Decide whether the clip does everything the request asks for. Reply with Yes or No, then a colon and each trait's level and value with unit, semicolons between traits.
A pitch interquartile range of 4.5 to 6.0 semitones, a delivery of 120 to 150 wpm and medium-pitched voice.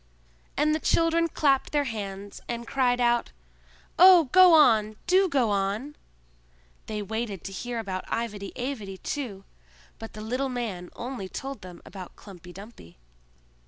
No: wide, 5.5 semitones; average, 145 wpm; high, 235 Hz